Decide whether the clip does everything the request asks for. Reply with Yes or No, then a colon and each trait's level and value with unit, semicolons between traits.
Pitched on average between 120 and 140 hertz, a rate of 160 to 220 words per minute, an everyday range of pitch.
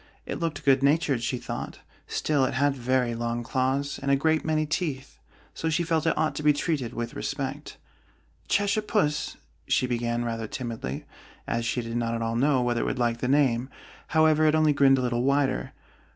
Yes: low, 135 Hz; average, 195 wpm; average, 4.3 semitones